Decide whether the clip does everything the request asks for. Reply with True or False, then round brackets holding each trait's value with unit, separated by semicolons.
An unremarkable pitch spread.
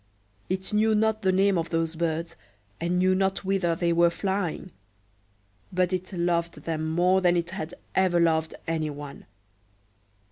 False (2.3 semitones)